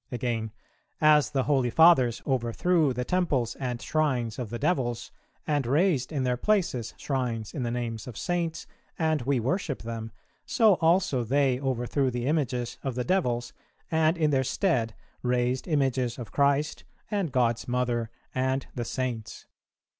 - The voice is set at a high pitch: No, low, 130 Hz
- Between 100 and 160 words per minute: Yes, average, 155 wpm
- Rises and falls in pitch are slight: No, average, 4.1 semitones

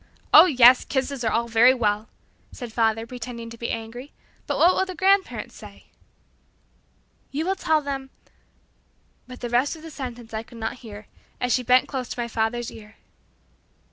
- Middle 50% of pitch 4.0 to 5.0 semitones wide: No, average, 3.0 semitones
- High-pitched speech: Yes, high, 245 Hz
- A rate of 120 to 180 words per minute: Yes, average, 175 wpm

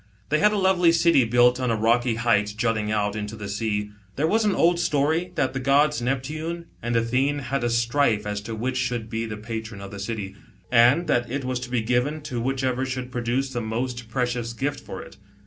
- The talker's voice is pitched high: No, low, 125 Hz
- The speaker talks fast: Yes, fast, 215 wpm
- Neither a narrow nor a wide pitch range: Yes, average, 3.5 semitones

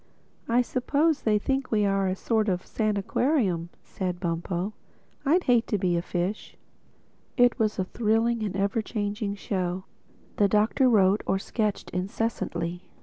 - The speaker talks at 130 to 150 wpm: Yes, average, 145 wpm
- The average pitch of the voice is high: Yes, high, 210 Hz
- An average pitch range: Yes, average, 3.6 semitones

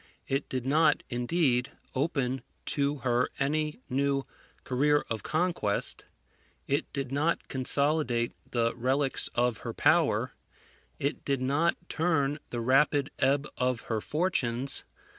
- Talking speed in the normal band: No, slow, 125 wpm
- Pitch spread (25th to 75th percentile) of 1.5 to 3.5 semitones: Yes, average, 2.9 semitones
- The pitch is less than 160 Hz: Yes, low, 135 Hz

